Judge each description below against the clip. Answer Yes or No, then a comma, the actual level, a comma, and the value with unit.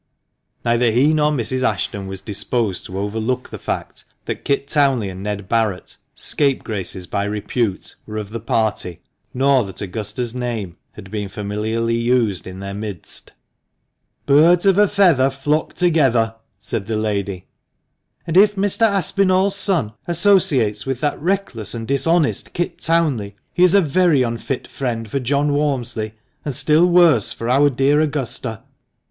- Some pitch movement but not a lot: No, wide, 6.1 semitones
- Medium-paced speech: Yes, average, 165 wpm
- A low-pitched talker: Yes, low, 125 Hz